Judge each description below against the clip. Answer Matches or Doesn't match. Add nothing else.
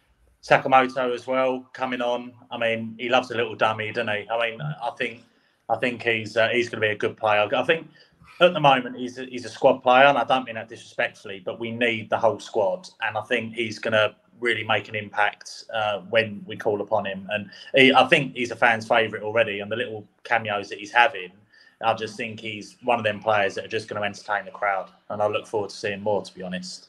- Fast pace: Matches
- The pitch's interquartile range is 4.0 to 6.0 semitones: Doesn't match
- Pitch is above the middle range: Doesn't match